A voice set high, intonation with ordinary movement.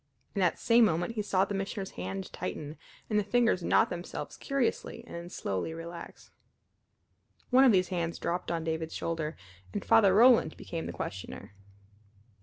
No: medium, 180 Hz; average, 4.6 semitones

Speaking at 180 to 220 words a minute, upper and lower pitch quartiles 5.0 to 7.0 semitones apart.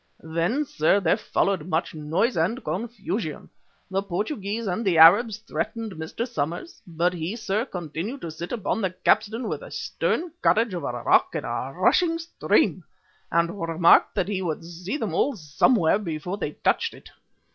No: average, 170 wpm; average, 5.3 semitones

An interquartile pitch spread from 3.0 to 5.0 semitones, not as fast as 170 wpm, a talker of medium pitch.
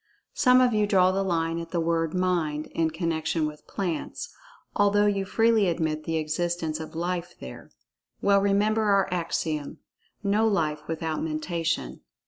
Yes: average, 3.7 semitones; average, 145 wpm; medium, 170 Hz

